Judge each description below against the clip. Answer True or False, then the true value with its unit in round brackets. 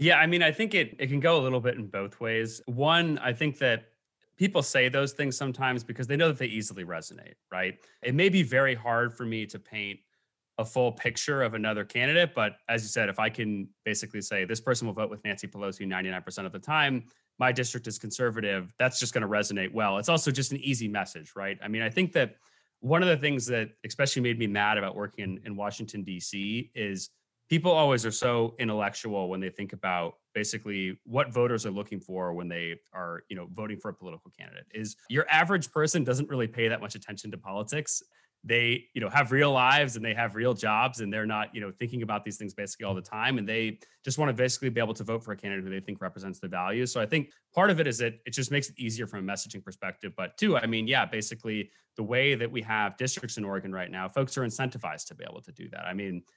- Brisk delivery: True (245 wpm)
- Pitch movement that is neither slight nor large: True (4.0 semitones)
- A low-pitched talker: True (115 Hz)